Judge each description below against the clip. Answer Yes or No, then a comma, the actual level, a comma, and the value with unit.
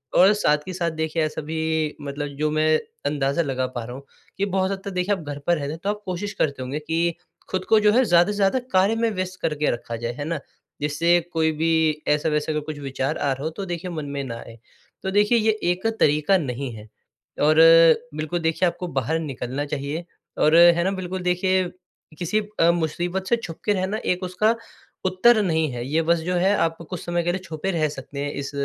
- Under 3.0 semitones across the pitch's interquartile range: No, average, 4.0 semitones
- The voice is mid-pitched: Yes, medium, 165 Hz